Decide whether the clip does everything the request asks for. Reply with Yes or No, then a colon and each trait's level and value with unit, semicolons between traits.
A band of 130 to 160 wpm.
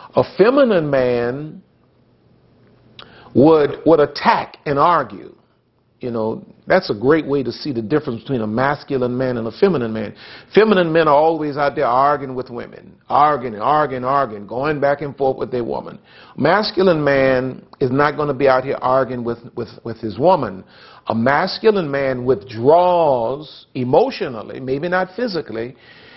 Yes: average, 155 wpm